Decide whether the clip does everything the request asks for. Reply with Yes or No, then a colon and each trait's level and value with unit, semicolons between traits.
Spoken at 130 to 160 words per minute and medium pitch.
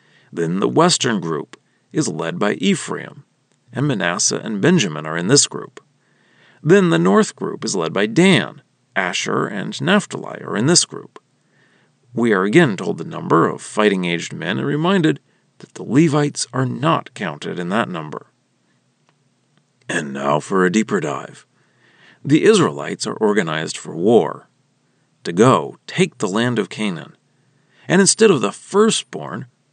Yes: average, 155 wpm; medium, 145 Hz